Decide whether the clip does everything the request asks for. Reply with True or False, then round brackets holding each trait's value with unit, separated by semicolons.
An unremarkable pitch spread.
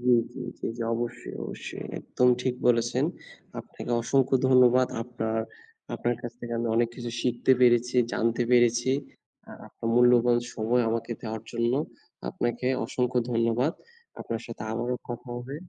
False (1.1 semitones)